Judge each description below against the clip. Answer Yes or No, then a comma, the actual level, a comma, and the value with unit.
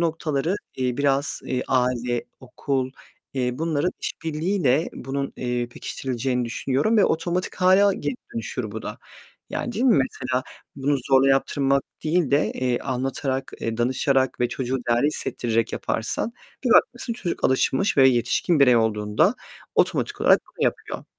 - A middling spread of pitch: Yes, average, 3.9 semitones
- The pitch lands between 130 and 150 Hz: Yes, low, 135 Hz